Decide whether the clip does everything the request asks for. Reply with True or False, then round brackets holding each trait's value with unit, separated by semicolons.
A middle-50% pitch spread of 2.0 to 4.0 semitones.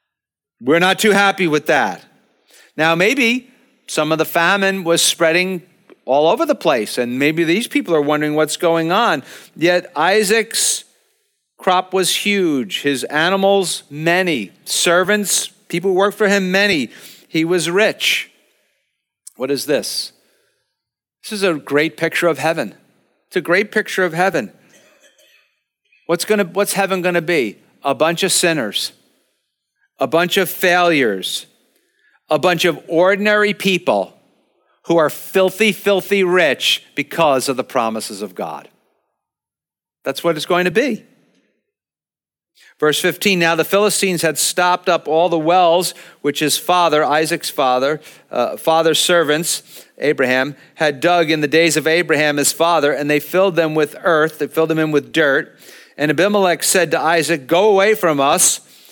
True (3.6 semitones)